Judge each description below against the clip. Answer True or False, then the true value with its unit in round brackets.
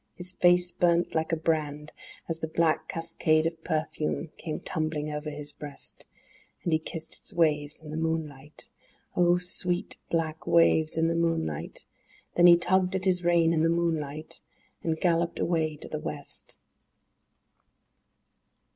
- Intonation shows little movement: True (1.8 semitones)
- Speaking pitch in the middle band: True (160 Hz)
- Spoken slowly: False (150 wpm)